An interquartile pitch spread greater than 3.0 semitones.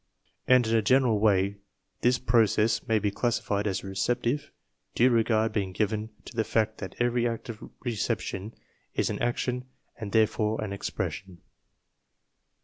No: narrow, 2.6 semitones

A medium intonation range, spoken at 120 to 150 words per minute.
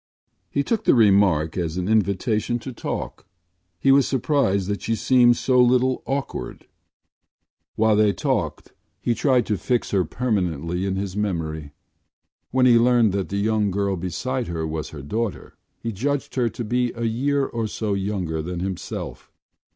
No: average, 4.9 semitones; average, 165 wpm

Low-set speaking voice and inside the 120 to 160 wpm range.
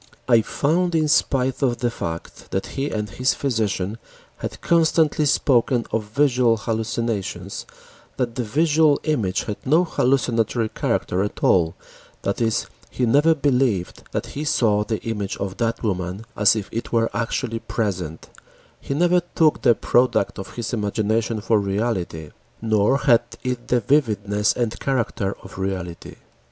Yes: low, 115 Hz; average, 150 wpm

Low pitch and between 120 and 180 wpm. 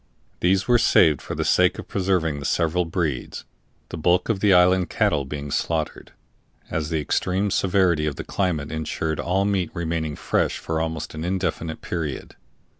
Yes: very low, 85 Hz; average, 170 wpm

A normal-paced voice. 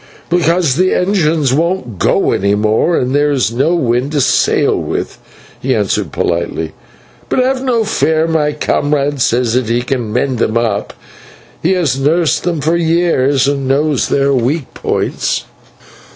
Yes: average, 155 wpm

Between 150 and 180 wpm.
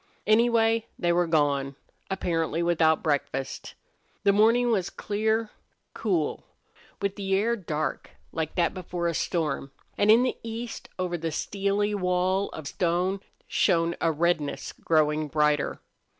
No: slow, 135 wpm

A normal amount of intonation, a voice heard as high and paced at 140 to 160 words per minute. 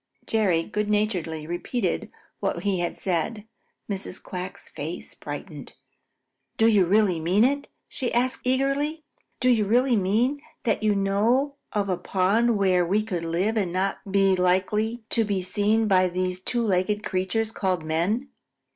Yes: average, 3.5 semitones; high, 205 Hz; average, 155 wpm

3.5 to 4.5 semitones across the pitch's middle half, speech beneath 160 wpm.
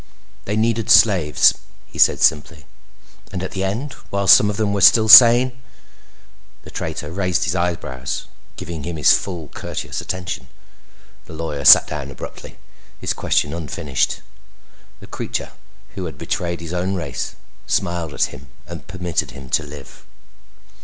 Yes: average, 4.1 semitones; average, 150 wpm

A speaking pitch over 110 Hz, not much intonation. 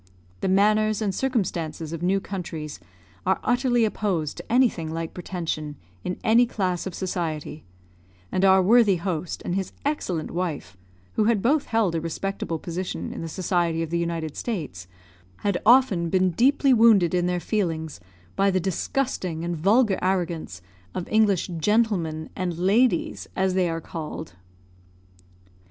No: medium, 185 Hz; average, 4.4 semitones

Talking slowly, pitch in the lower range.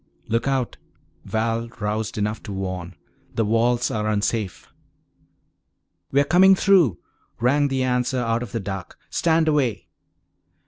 Yes: slow, 130 wpm; low, 115 Hz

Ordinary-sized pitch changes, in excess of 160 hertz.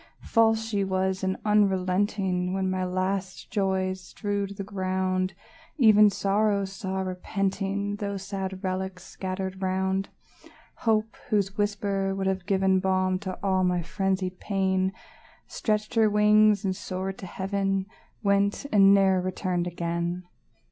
No: narrow, 1.3 semitones; high, 190 Hz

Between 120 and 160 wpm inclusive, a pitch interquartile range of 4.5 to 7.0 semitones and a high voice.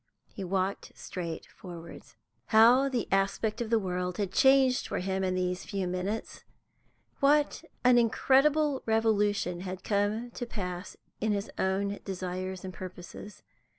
No: average, 140 wpm; average, 3.8 semitones; high, 200 Hz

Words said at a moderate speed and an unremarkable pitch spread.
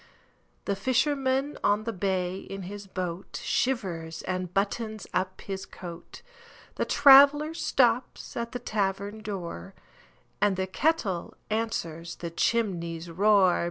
No: slow, 110 wpm; average, 4.6 semitones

